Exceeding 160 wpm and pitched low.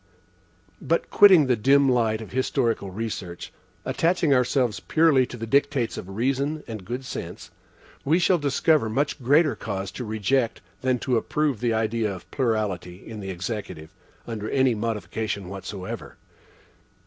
No: average, 145 wpm; low, 115 Hz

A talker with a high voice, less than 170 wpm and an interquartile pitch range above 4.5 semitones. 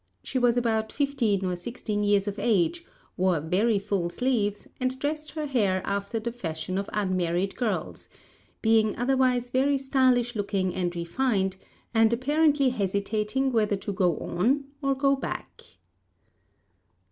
Yes: high, 220 Hz; average, 140 wpm; average, 5.0 semitones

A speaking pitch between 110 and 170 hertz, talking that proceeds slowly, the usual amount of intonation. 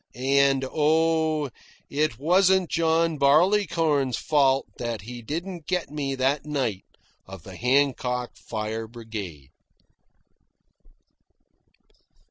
Yes: medium, 140 Hz; slow, 95 wpm; average, 5.0 semitones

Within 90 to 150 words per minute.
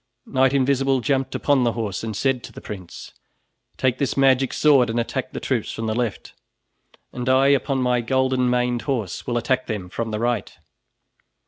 No: average, 185 wpm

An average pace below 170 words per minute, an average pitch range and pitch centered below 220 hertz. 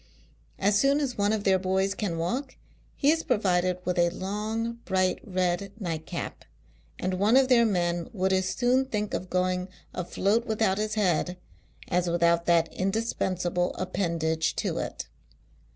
Yes: average, 150 wpm; average, 3.4 semitones; high, 190 Hz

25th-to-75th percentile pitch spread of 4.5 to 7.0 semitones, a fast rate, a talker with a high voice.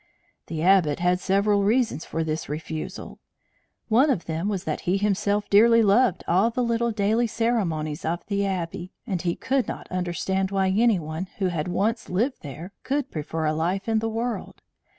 No: average, 4.8 semitones; average, 180 wpm; high, 195 Hz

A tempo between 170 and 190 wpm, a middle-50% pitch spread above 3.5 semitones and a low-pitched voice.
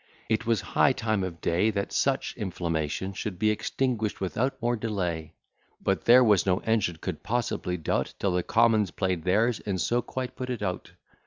Yes: average, 180 wpm; average, 4.3 semitones; low, 105 Hz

